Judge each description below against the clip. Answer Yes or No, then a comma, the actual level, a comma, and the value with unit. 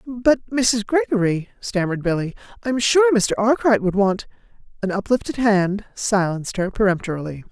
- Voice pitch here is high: Yes, high, 215 Hz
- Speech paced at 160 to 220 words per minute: No, average, 145 wpm